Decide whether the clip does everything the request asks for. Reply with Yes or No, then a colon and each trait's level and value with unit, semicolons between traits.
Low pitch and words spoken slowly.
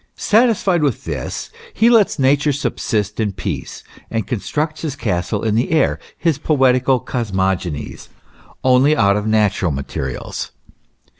Yes: low, 120 Hz; slow, 130 wpm